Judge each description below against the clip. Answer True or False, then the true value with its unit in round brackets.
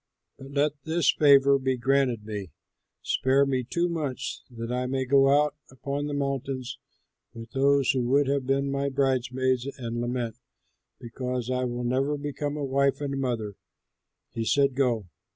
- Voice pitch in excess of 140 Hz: False (135 Hz)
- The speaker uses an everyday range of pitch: False (2.0 semitones)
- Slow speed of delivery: False (160 wpm)